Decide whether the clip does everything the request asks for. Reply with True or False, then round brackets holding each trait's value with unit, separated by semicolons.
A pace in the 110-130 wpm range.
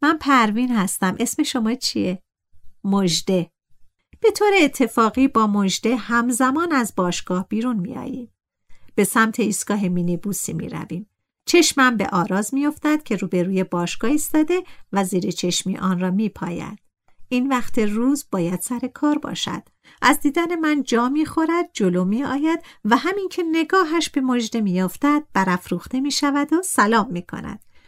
False (155 wpm)